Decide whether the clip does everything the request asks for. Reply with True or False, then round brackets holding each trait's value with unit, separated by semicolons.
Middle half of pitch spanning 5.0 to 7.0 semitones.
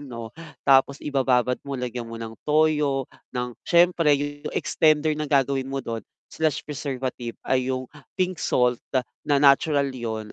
False (3.1 semitones)